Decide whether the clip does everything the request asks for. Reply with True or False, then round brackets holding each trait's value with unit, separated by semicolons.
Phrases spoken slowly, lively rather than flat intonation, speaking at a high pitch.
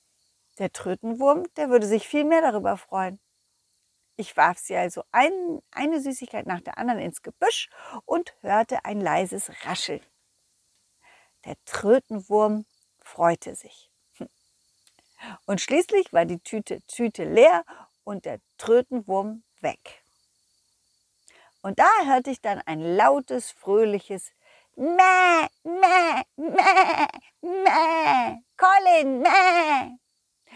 True (110 wpm; 8.5 semitones; 260 Hz)